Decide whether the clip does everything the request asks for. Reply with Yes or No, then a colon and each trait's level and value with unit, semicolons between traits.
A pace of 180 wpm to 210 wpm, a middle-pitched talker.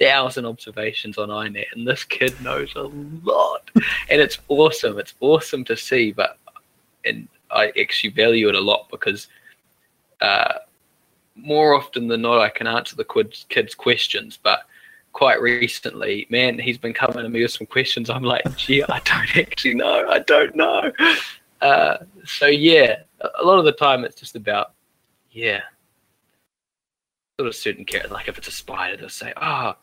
No: average, 170 wpm; medium, 145 Hz